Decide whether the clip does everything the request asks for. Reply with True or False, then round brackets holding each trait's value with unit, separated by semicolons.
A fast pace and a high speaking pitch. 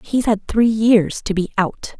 True (210 wpm; 210 Hz)